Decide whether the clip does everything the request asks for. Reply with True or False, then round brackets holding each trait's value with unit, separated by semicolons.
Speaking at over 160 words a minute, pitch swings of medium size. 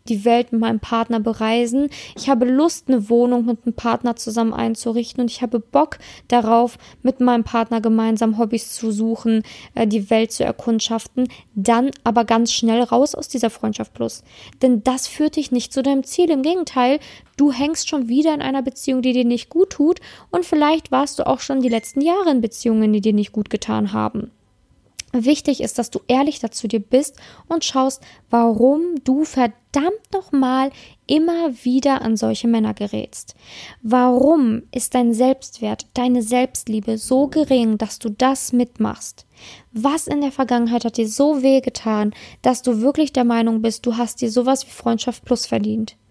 True (175 wpm; 3.0 semitones)